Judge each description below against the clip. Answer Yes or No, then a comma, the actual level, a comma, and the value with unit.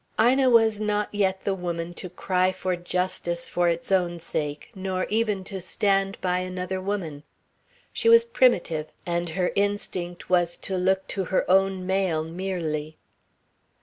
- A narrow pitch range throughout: Yes, narrow, 2.1 semitones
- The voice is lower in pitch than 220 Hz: Yes, medium, 185 Hz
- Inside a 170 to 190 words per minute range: No, average, 150 wpm